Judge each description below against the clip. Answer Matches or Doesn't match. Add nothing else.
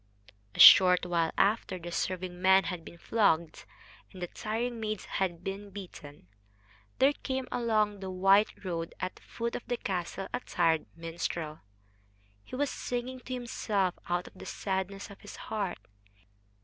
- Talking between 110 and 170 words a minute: Matches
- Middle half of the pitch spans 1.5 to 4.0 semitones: Matches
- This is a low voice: Doesn't match